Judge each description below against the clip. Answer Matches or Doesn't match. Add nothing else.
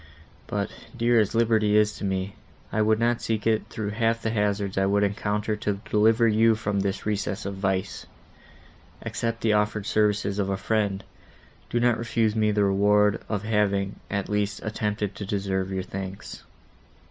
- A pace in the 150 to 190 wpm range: Matches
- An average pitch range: Doesn't match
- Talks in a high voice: Doesn't match